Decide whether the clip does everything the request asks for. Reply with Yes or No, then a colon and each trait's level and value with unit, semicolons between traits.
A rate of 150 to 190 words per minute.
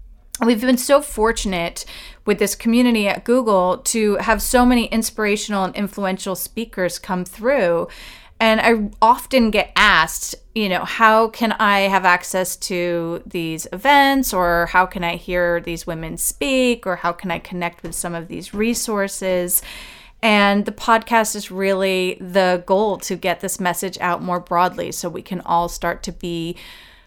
Yes: average, 160 wpm